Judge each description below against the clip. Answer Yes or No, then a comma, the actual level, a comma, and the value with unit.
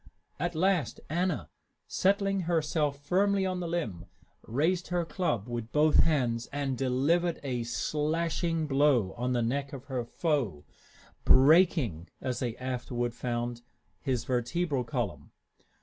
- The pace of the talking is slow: Yes, slow, 130 wpm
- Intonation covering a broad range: Yes, wide, 5.7 semitones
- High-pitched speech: No, medium, 140 Hz